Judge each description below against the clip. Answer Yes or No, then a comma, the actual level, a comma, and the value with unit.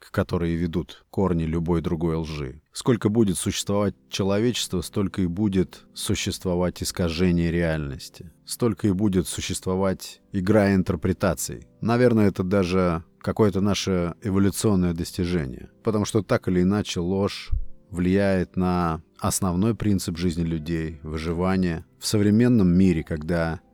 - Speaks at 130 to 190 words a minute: No, average, 115 wpm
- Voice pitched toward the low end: Yes, very low, 95 Hz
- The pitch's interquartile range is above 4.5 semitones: No, average, 2.8 semitones